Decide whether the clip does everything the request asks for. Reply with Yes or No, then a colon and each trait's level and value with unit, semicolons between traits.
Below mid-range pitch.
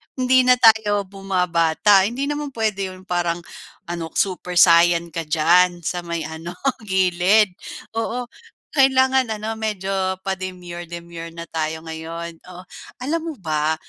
No: medium, 180 Hz